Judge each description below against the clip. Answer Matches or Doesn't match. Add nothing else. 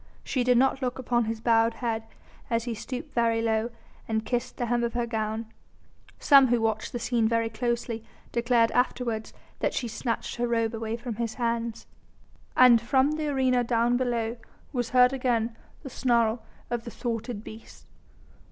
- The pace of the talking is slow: Doesn't match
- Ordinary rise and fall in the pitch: Doesn't match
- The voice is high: Matches